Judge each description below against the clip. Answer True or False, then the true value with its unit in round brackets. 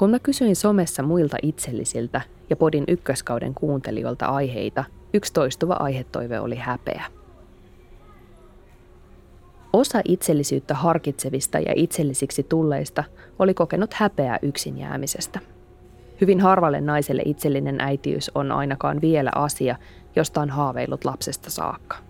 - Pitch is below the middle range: False (145 Hz)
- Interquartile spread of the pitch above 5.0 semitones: True (5.5 semitones)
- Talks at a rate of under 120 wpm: True (110 wpm)